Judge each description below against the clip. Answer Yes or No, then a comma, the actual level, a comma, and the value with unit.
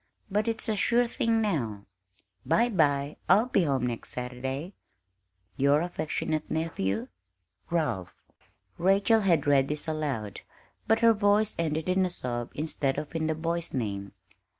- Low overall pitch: No, medium, 160 Hz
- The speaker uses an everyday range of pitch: No, wide, 6.9 semitones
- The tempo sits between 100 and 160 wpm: Yes, average, 145 wpm